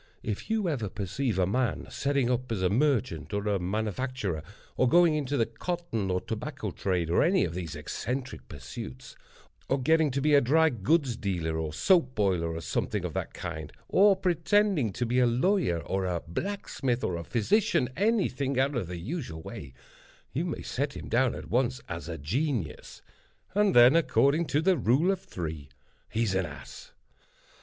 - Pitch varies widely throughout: Yes, wide, 8.6 semitones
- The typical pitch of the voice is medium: No, low, 125 Hz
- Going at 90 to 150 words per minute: No, average, 175 wpm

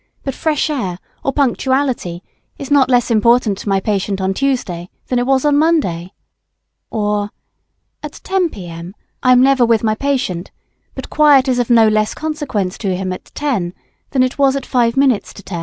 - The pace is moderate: Yes, average, 185 wpm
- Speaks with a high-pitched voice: Yes, high, 245 Hz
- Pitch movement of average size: No, wide, 5.7 semitones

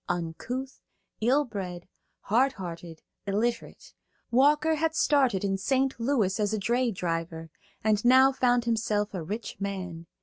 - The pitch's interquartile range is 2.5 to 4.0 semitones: No, wide, 5.6 semitones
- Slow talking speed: Yes, slow, 130 wpm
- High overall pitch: Yes, high, 215 Hz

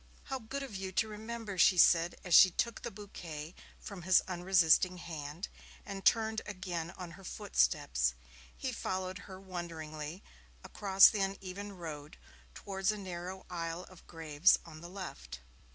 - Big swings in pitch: No, average, 3.0 semitones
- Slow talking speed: No, average, 150 wpm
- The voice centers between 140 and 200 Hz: Yes, medium, 185 Hz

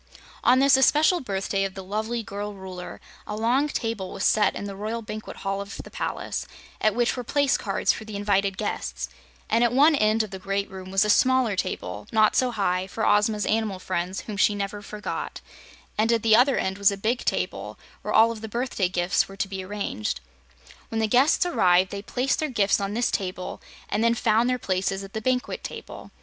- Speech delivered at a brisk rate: Yes, fast, 215 wpm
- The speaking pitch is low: No, high, 210 Hz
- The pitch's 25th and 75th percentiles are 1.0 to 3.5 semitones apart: Yes, average, 3.1 semitones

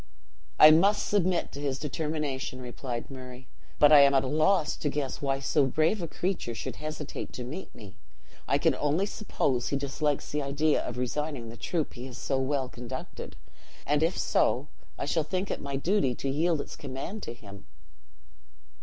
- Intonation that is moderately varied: Yes, average, 3.2 semitones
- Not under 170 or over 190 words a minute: Yes, average, 185 wpm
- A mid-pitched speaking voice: Yes, medium, 145 Hz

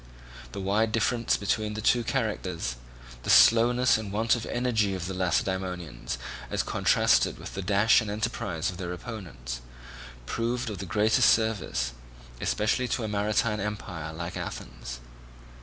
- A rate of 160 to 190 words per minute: No, average, 145 wpm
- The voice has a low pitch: Yes, low, 105 Hz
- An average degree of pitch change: Yes, average, 3.9 semitones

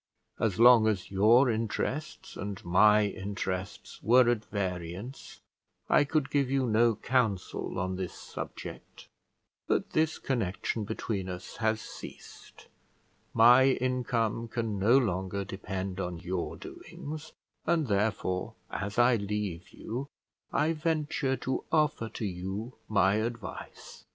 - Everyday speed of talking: No, slow, 125 wpm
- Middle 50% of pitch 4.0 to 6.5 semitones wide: Yes, average, 4.6 semitones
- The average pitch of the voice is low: Yes, low, 110 Hz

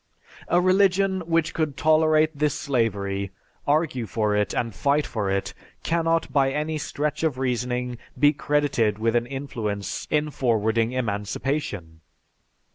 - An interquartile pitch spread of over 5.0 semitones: Yes, wide, 5.5 semitones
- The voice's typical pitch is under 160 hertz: Yes, low, 135 Hz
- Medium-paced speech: No, slow, 130 wpm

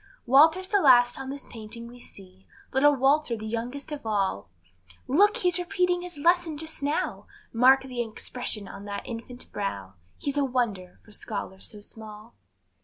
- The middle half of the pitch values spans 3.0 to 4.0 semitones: No, average, 5.3 semitones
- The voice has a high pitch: Yes, very high, 250 Hz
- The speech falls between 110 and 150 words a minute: No, average, 165 wpm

